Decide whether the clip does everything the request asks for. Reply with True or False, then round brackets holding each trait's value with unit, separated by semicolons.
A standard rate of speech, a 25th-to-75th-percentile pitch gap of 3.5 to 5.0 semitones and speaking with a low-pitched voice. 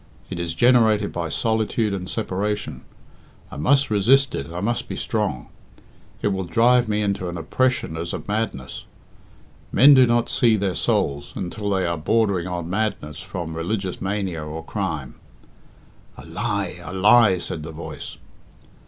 True (155 wpm; 4.6 semitones; 95 Hz)